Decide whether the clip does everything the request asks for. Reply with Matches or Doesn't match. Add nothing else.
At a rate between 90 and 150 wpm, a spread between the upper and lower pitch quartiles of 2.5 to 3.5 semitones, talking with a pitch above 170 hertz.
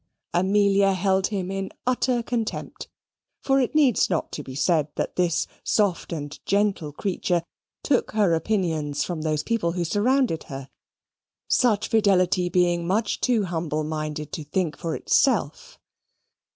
Doesn't match